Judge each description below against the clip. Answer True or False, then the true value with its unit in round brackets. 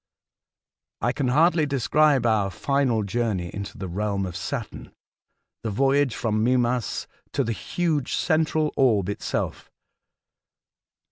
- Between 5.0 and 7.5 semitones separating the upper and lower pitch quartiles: True (5.5 semitones)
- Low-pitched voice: True (120 Hz)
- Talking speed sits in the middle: False (125 wpm)